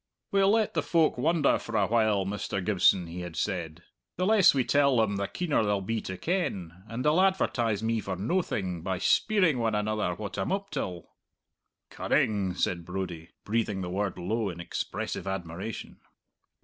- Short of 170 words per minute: No, average, 175 wpm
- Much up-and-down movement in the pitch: Yes, wide, 7.0 semitones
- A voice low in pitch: Yes, low, 105 Hz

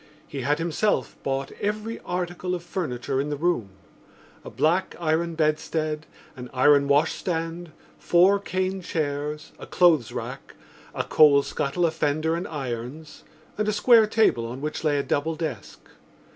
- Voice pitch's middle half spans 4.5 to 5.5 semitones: No, average, 3.6 semitones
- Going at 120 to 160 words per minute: Yes, average, 150 wpm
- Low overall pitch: No, medium, 155 Hz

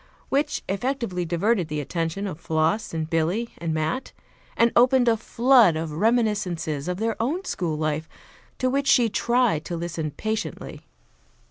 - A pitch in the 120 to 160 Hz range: No, high, 190 Hz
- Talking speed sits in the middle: Yes, average, 150 wpm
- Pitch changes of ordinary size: No, wide, 6.6 semitones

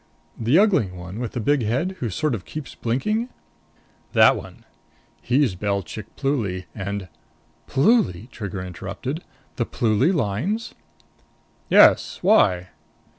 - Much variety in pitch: Yes, wide, 6.9 semitones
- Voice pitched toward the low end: Yes, low, 115 Hz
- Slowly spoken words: Yes, slow, 125 wpm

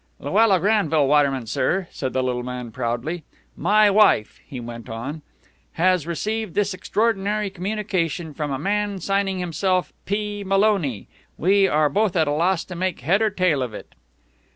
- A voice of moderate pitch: Yes, medium, 180 Hz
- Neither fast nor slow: Yes, average, 160 wpm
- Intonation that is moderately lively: No, wide, 6.0 semitones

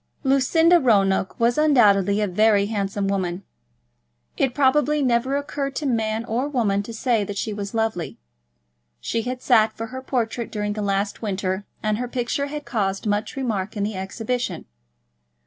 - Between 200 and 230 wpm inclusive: No, average, 165 wpm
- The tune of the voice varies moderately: Yes, average, 4.1 semitones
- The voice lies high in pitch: Yes, high, 225 Hz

